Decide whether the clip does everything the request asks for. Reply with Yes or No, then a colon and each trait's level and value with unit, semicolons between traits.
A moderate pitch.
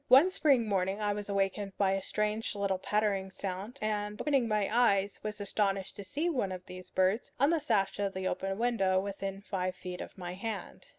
No: high, 200 Hz